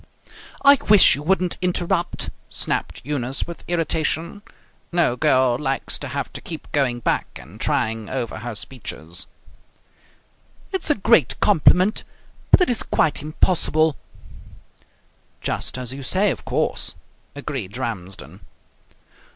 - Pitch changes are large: Yes, wide, 6.5 semitones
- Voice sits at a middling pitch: Yes, medium, 145 Hz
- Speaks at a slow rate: Yes, slow, 125 wpm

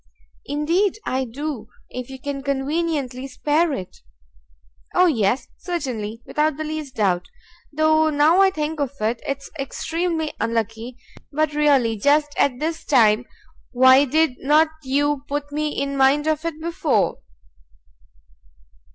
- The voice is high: Yes, very high, 285 Hz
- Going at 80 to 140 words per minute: Yes, slow, 135 wpm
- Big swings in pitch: No, average, 3.4 semitones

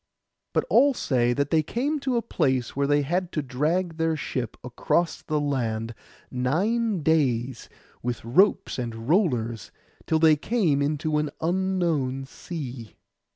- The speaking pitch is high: No, medium, 150 Hz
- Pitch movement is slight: No, wide, 5.6 semitones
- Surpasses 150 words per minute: No, average, 145 wpm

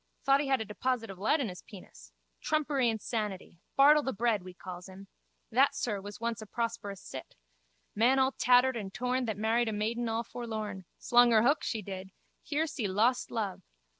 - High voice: Yes, high, 225 Hz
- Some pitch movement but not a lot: Yes, average, 3.7 semitones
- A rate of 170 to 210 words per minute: Yes, average, 195 wpm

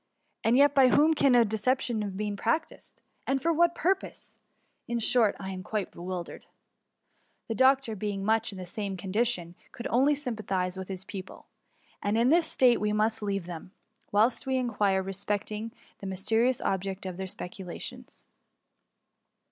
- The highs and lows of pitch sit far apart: No, average, 4.4 semitones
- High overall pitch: Yes, high, 215 Hz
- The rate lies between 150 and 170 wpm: Yes, average, 165 wpm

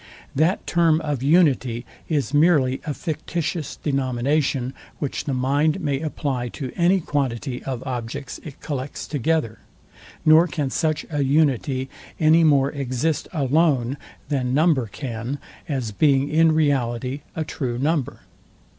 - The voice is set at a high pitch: No, medium, 140 Hz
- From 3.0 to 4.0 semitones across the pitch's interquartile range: Yes, average, 3.3 semitones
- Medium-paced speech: No, slow, 130 wpm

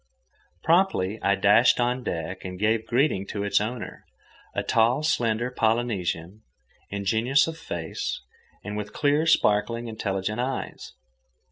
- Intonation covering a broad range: No, average, 3.8 semitones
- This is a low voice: Yes, low, 110 Hz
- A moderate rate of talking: No, slow, 125 wpm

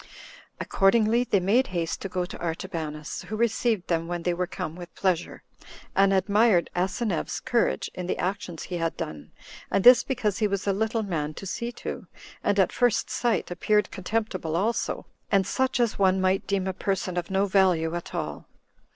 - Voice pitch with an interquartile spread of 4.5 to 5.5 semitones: No, average, 3.4 semitones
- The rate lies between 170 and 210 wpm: Yes, average, 185 wpm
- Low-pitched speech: No, high, 190 Hz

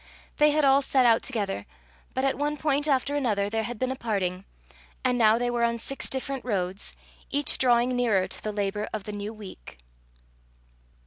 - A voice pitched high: Yes, high, 235 Hz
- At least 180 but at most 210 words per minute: Yes, average, 190 wpm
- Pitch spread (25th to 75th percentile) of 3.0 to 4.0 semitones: No, average, 4.4 semitones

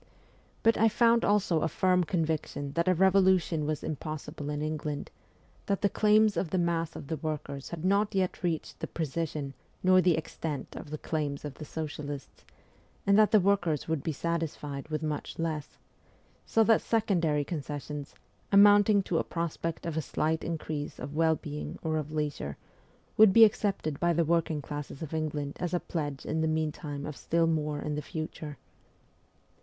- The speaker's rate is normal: Yes, average, 175 wpm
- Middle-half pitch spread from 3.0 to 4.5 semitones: Yes, average, 3.4 semitones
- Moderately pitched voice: Yes, medium, 160 Hz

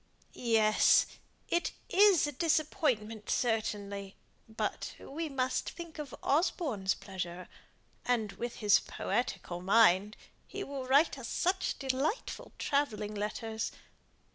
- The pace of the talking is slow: Yes, slow, 110 wpm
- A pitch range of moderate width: No, wide, 5.9 semitones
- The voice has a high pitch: Yes, high, 240 Hz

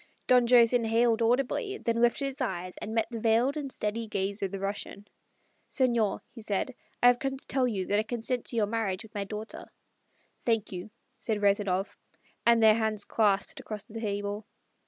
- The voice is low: No, high, 225 Hz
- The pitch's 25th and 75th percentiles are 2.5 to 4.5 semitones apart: Yes, average, 2.8 semitones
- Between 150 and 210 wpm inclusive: Yes, average, 190 wpm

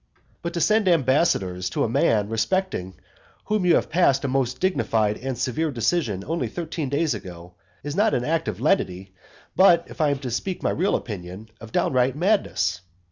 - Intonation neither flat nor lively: No, wide, 7.8 semitones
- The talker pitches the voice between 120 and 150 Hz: Yes, low, 135 Hz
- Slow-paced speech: No, average, 185 wpm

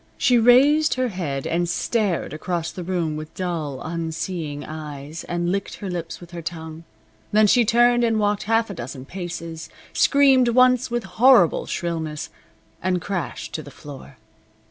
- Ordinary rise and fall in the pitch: No, wide, 5.9 semitones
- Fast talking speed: No, average, 160 wpm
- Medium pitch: Yes, medium, 175 Hz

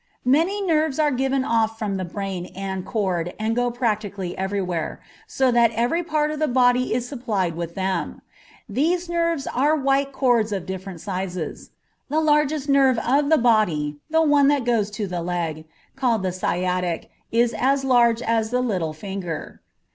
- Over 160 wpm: Yes, average, 170 wpm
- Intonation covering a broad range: Yes, wide, 6.4 semitones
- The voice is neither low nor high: No, high, 230 Hz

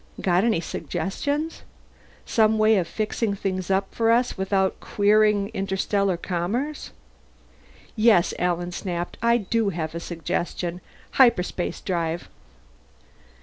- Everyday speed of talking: No, slow, 110 wpm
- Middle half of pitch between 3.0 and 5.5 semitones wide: Yes, average, 3.8 semitones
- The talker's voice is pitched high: Yes, high, 195 Hz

